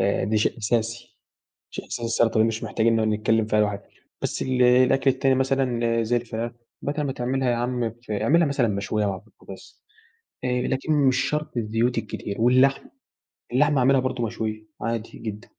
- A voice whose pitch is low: Yes, low, 120 Hz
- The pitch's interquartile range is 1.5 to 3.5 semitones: Yes, average, 3.0 semitones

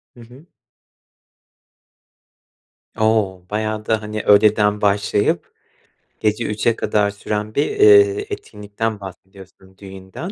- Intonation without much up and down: Yes, narrow, 1.8 semitones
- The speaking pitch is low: Yes, low, 105 Hz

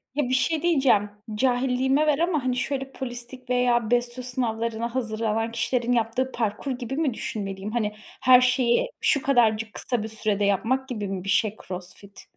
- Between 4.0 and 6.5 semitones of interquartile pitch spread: No, average, 3.0 semitones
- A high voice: Yes, high, 245 Hz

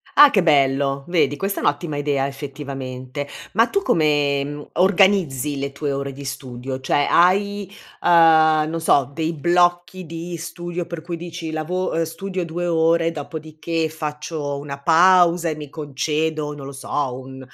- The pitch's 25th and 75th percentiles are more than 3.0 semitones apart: Yes, average, 3.5 semitones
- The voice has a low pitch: No, medium, 155 Hz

